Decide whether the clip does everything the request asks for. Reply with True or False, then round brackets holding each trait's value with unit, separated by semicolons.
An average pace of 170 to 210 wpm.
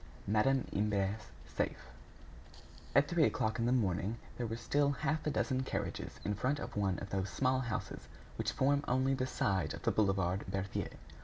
True (175 wpm)